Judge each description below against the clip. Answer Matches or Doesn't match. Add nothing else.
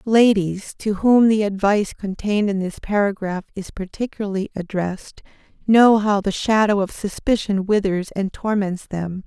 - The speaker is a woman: Matches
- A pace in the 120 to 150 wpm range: Matches